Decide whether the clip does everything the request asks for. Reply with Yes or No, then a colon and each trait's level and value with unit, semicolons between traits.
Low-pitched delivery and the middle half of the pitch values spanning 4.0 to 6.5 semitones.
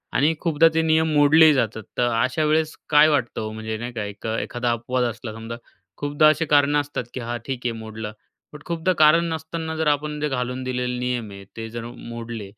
Yes: low, 130 Hz; average, 4.6 semitones